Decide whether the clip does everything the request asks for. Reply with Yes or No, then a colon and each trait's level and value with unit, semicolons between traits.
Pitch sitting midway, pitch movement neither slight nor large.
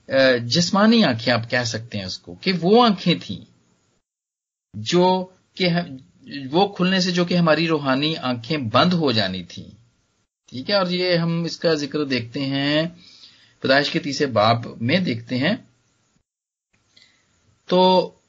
No: medium, 145 Hz; wide, 6.8 semitones